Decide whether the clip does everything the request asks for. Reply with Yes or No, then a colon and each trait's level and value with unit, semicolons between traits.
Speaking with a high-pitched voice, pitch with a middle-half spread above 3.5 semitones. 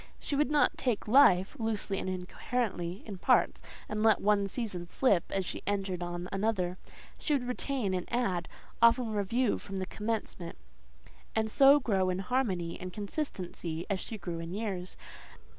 Yes: high, 200 Hz; average, 4.3 semitones